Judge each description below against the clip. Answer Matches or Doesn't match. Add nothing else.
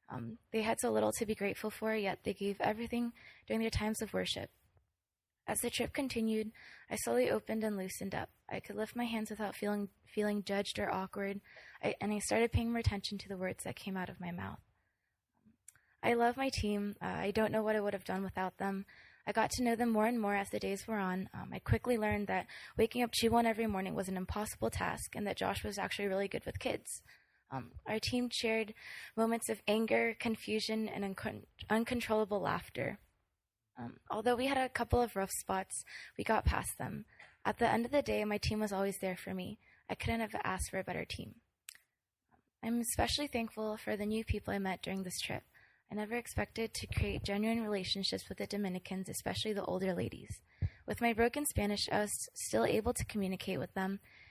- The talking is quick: Matches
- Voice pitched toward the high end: Matches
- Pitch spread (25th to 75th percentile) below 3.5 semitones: Matches